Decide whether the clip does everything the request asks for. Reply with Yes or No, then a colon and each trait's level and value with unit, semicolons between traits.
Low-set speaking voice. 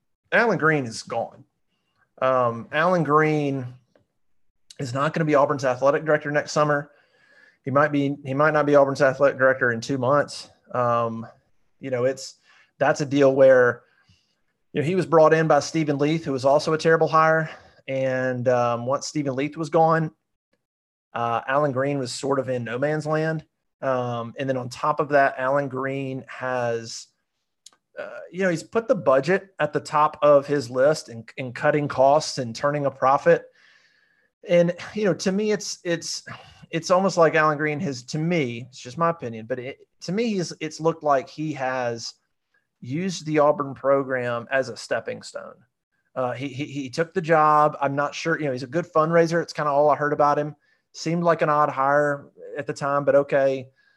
No: medium, 145 Hz